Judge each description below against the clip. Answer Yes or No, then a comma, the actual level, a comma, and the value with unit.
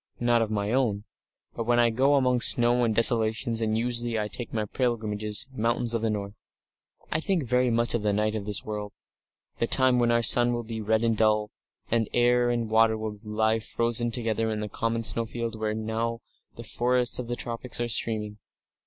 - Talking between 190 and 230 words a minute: Yes, fast, 205 wpm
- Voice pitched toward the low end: Yes, low, 115 Hz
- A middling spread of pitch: No, narrow, 1.7 semitones